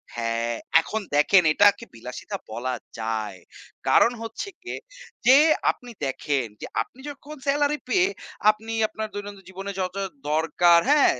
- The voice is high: Yes, high, 195 Hz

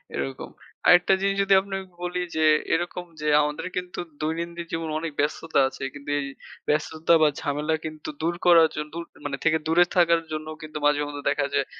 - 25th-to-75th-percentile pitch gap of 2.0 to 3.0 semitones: Yes, narrow, 2.6 semitones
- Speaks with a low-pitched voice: No, medium, 160 Hz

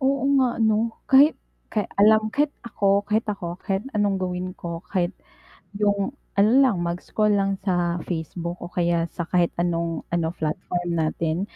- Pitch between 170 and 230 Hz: Yes, high, 190 Hz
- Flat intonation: No, average, 3.6 semitones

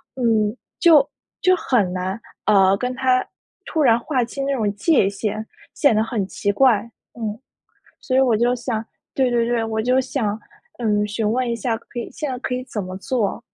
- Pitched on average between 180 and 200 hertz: No, high, 235 Hz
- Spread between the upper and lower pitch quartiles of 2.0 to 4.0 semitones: Yes, average, 3.4 semitones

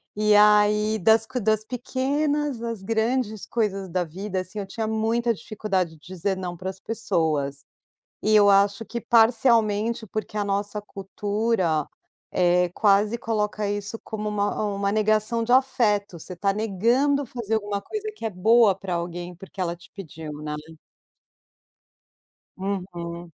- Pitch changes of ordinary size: Yes, average, 3.0 semitones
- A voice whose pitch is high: Yes, high, 210 Hz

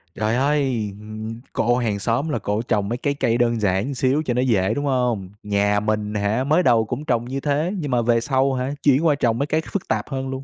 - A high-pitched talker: No, low, 120 Hz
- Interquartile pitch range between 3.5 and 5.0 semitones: Yes, average, 4.1 semitones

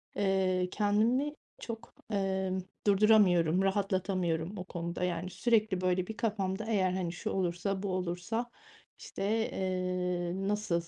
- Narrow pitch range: Yes, narrow, 2.2 semitones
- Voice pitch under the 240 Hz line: Yes, high, 190 Hz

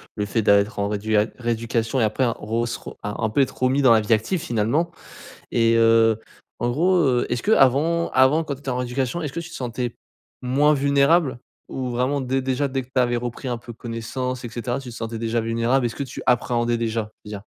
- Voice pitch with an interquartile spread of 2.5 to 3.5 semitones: Yes, average, 2.8 semitones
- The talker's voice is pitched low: Yes, low, 120 Hz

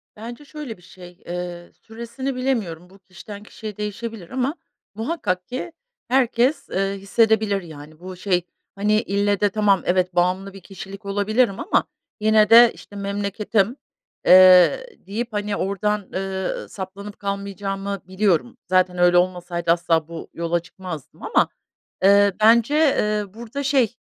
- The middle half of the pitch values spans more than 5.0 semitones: No, average, 3.3 semitones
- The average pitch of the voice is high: Yes, high, 200 Hz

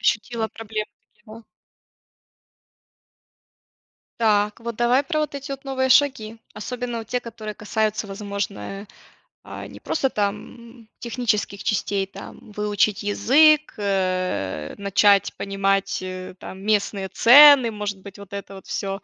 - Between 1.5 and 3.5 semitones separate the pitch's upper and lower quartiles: Yes, average, 3.1 semitones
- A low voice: No, high, 210 Hz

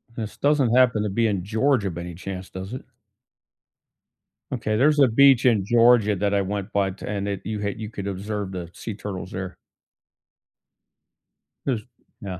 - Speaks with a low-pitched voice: Yes, low, 105 Hz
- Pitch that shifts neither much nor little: Yes, average, 3.3 semitones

